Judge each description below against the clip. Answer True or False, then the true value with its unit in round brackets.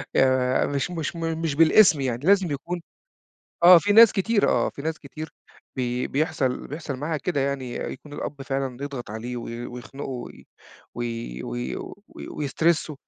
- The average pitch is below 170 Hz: True (140 Hz)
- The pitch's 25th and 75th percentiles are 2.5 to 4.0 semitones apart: False (4.4 semitones)